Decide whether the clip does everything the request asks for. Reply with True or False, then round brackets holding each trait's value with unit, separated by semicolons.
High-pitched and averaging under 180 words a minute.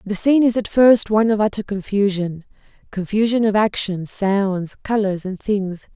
True (205 Hz; 150 wpm)